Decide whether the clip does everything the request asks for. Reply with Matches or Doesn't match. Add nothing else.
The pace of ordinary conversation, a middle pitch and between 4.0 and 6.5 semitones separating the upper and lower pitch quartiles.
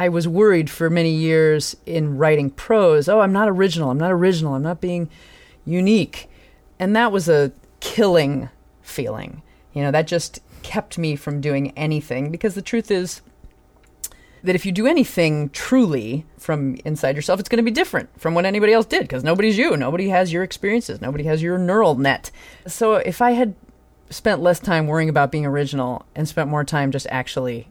Matches